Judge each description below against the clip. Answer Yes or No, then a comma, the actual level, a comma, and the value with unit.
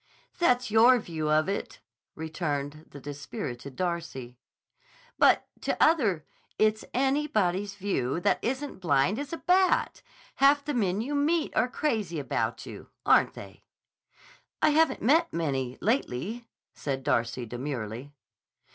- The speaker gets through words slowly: Yes, slow, 130 wpm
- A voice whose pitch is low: No, medium, 185 Hz